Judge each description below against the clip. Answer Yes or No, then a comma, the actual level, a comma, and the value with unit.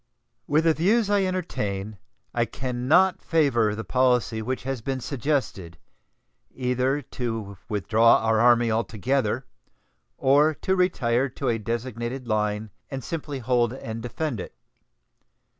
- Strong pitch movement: No, average, 3.9 semitones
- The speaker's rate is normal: No, slow, 130 wpm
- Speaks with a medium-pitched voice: No, low, 125 Hz